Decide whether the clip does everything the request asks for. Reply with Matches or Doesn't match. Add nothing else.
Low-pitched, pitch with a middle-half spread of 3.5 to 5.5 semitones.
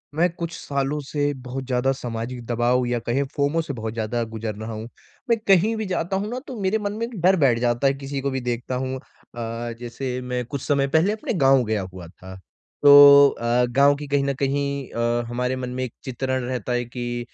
Doesn't match